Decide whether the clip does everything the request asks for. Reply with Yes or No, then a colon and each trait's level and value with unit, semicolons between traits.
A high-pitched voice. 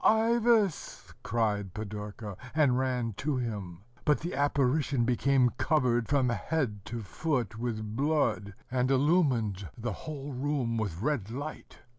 No: low, 125 Hz